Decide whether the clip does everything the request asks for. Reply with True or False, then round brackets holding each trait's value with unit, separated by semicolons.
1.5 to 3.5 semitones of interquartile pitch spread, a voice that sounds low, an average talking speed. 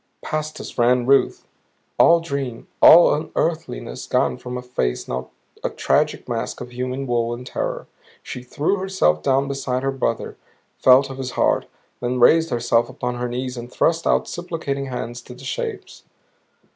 True (2.5 semitones; 125 Hz; 165 wpm)